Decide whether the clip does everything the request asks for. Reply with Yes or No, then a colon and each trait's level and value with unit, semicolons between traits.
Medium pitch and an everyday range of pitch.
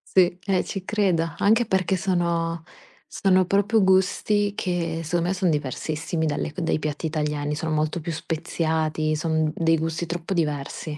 Yes: medium, 165 Hz; average, 3.1 semitones